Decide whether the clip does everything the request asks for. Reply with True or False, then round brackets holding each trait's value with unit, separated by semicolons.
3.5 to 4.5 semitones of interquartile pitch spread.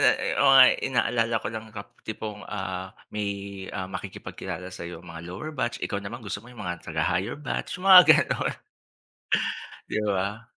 True (3.9 semitones)